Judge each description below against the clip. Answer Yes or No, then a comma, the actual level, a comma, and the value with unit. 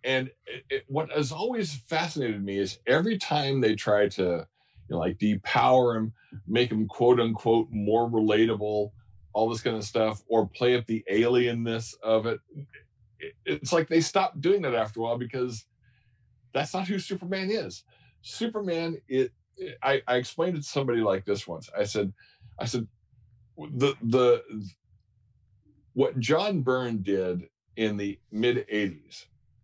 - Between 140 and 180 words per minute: Yes, average, 160 wpm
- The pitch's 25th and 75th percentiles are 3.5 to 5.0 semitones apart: Yes, average, 4.3 semitones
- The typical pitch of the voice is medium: No, low, 120 Hz